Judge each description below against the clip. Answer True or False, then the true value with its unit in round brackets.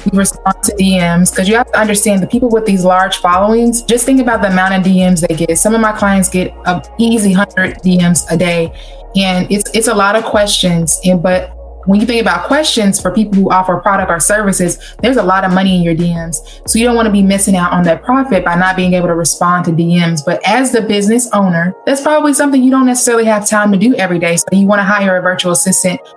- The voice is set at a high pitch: True (195 Hz)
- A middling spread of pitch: True (3.3 semitones)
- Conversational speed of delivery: False (250 wpm)